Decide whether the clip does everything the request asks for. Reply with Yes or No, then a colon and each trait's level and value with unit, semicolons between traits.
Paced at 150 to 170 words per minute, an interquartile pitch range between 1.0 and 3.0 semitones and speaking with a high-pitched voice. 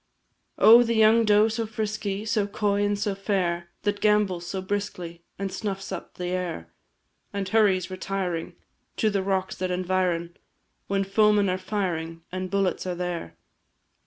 Yes: average, 155 wpm; narrow, 2.4 semitones; high, 195 Hz